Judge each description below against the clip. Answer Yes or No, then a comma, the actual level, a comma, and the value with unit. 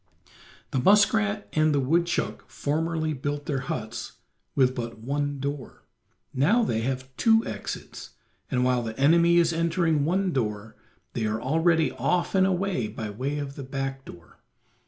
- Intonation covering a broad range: No, average, 4.8 semitones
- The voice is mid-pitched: Yes, medium, 145 Hz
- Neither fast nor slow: Yes, average, 155 wpm